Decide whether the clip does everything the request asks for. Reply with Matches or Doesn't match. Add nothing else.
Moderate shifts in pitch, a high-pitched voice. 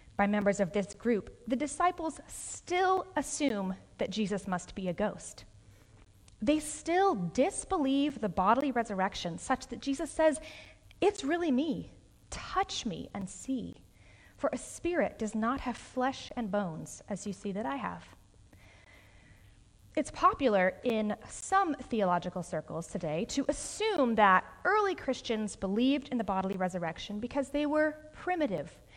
Doesn't match